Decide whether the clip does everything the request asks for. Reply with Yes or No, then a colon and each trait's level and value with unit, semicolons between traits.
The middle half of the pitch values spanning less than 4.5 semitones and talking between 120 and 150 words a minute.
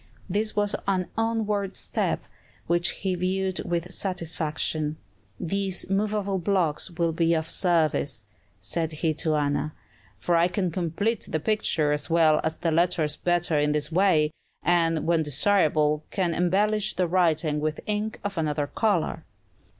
Yes: average, 3.7 semitones; average, 145 wpm